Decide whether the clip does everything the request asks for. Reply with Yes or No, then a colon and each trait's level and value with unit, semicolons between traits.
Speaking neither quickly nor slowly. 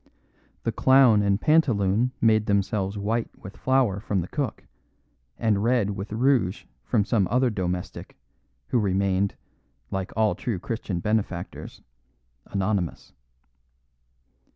No: slow, 115 wpm